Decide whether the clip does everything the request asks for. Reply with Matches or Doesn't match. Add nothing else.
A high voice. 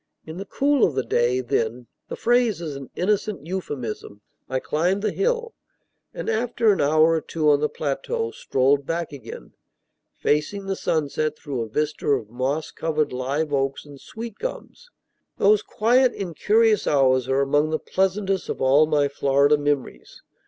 Doesn't match